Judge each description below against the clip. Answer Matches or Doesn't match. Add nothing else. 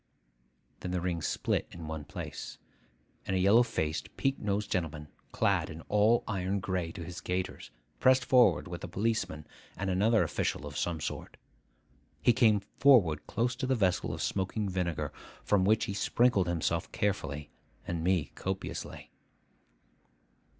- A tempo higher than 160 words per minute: Doesn't match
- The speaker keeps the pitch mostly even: Doesn't match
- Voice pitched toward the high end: Doesn't match